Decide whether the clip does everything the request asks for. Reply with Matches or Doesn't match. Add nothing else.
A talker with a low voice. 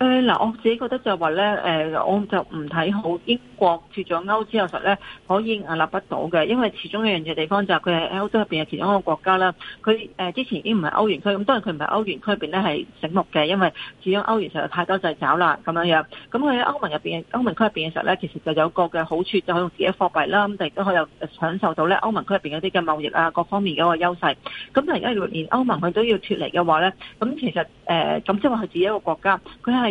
Doesn't match